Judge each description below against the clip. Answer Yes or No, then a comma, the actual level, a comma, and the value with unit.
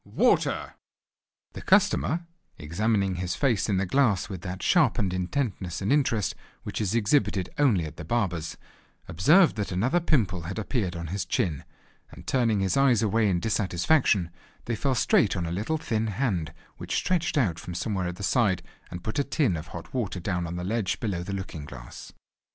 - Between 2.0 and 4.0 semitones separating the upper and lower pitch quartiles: No, average, 5.2 semitones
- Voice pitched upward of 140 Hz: No, low, 100 Hz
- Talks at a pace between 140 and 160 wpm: No, average, 185 wpm